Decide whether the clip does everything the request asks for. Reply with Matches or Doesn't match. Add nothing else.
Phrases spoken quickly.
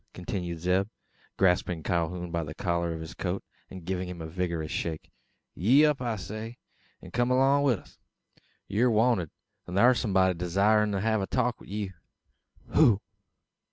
Doesn't match